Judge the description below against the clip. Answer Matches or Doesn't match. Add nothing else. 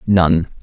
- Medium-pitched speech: Doesn't match